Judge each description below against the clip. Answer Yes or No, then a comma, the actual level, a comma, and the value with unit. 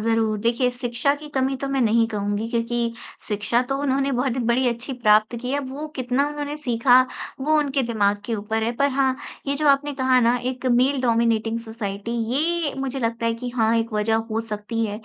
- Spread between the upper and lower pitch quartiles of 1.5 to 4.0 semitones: Yes, average, 3.0 semitones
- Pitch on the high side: Yes, high, 240 Hz